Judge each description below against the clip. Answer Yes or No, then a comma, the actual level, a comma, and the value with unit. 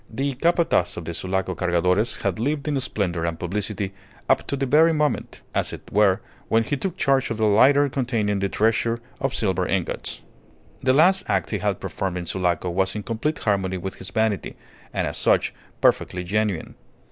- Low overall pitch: Yes, low, 105 Hz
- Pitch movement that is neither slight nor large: No, wide, 6.4 semitones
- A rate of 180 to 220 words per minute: Yes, average, 185 wpm